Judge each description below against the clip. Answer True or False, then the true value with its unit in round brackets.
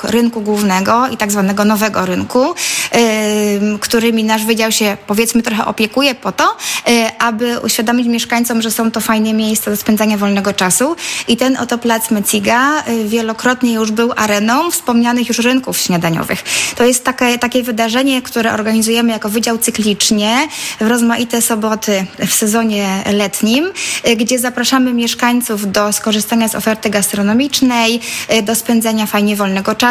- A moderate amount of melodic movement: False (2.0 semitones)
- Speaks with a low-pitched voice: False (230 Hz)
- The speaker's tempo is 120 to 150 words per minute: True (140 wpm)